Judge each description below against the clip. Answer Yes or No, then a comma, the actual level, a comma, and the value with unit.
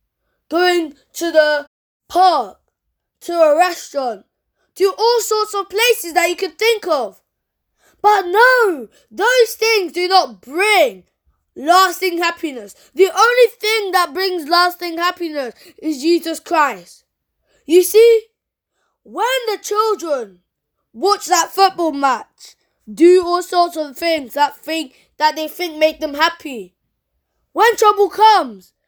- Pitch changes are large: No, average, 4.7 semitones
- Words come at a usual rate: No, slow, 125 wpm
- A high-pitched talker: Yes, very high, 350 Hz